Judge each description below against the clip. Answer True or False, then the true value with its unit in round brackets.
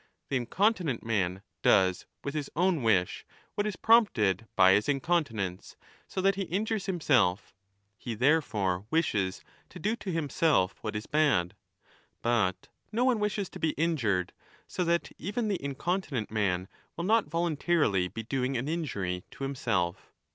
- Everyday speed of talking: True (160 wpm)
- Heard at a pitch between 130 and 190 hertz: True (135 Hz)